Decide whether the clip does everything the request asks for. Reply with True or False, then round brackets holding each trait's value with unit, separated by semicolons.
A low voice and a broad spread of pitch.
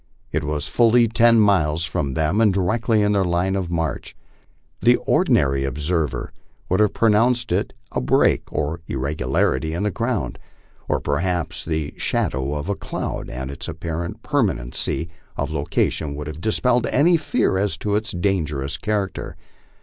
True (85 Hz; 6.1 semitones)